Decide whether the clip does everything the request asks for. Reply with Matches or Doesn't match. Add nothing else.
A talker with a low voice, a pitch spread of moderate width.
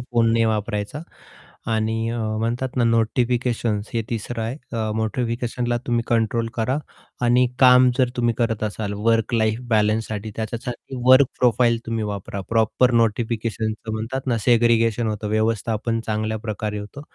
Doesn't match